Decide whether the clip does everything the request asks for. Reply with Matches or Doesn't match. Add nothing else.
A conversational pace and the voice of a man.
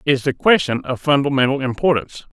Matches